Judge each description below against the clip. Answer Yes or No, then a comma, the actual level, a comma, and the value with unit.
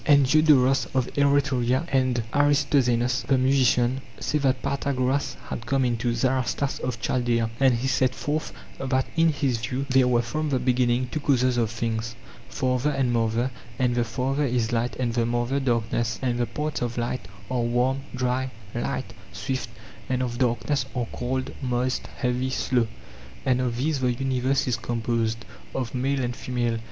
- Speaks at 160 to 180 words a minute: Yes, average, 170 wpm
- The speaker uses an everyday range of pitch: No, narrow, 1.9 semitones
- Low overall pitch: Yes, low, 125 Hz